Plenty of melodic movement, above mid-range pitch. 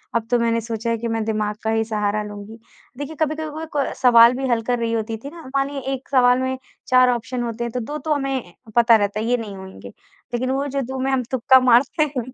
No: average, 2.9 semitones; high, 245 Hz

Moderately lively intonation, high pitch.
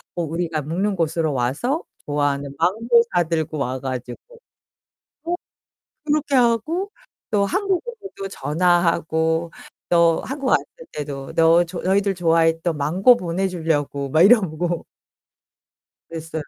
No: average, 4.5 semitones; medium, 170 Hz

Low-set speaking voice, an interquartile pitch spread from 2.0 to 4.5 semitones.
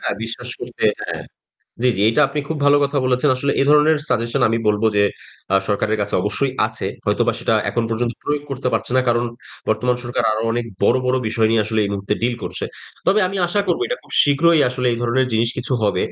Yes: low, 120 Hz; average, 3.8 semitones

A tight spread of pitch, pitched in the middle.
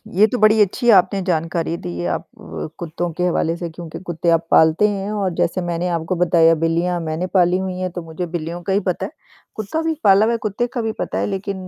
No: average, 3.0 semitones; medium, 180 Hz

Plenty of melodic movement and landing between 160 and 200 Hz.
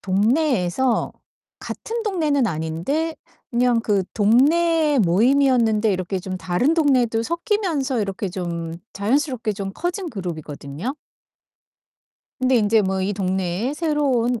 No: wide, 7.2 semitones; high, 230 Hz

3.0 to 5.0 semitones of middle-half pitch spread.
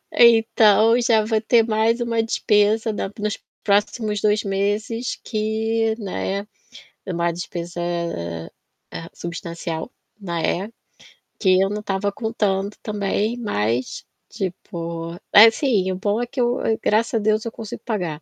Yes: average, 3.5 semitones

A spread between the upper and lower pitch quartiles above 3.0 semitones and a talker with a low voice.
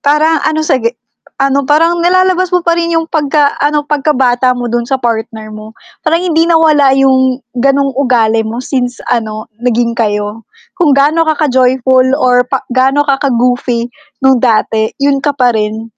No: average, 3.9 semitones; very high, 265 Hz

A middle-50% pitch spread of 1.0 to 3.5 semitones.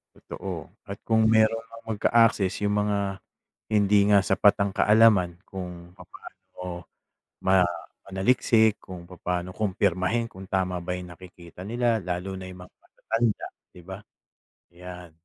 Yes: average, 2.9 semitones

